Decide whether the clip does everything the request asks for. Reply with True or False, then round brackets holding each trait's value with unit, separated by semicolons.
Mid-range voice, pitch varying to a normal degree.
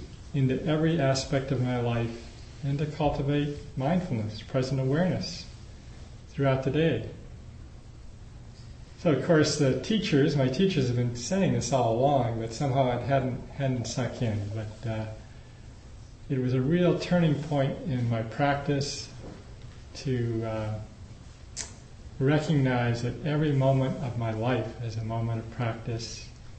False (130 Hz; 3.8 semitones)